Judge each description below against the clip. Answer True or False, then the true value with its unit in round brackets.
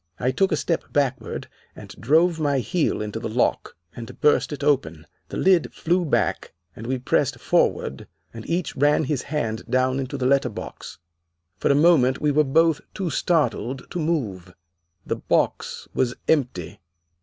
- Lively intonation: False (4.5 semitones)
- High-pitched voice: False (135 Hz)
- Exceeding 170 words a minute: False (165 wpm)